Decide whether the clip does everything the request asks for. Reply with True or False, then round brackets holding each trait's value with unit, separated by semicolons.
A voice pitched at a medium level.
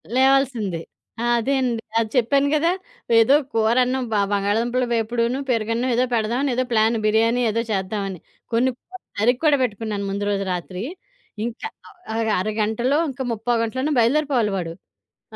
False (230 Hz)